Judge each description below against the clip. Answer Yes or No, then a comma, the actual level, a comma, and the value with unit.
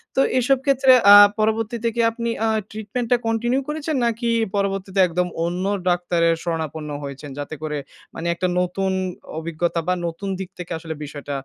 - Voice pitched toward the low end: No, high, 190 Hz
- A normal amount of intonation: No, wide, 5.7 semitones